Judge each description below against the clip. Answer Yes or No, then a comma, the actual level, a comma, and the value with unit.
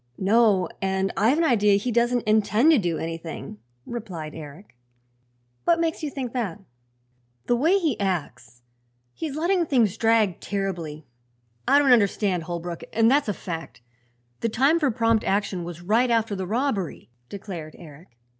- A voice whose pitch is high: Yes, high, 210 Hz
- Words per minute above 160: No, average, 155 wpm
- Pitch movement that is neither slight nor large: No, wide, 5.8 semitones